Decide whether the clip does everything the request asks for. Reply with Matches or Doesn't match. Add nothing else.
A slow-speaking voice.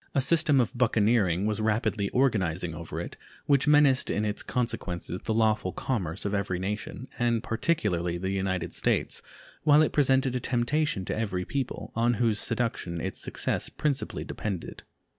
Doesn't match